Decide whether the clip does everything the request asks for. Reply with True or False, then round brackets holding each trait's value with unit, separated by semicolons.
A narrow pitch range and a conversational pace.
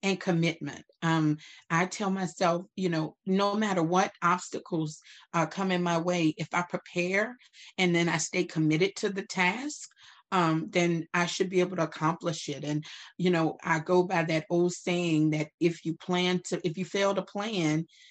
True (2.2 semitones; 185 wpm)